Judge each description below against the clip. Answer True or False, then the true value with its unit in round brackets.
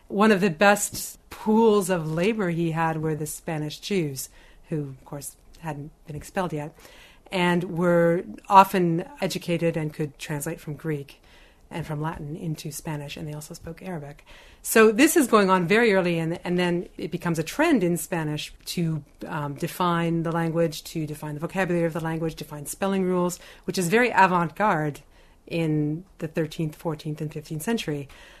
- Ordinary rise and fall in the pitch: True (3.1 semitones)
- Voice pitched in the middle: True (170 Hz)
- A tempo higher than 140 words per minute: True (170 wpm)